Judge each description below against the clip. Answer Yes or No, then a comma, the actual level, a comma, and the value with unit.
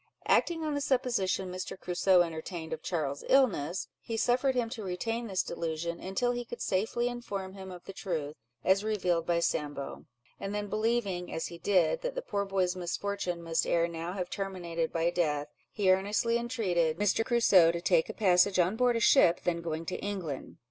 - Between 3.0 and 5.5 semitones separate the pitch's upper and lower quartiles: Yes, average, 4.8 semitones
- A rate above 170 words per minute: Yes, average, 190 wpm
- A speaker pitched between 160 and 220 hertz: Yes, high, 190 Hz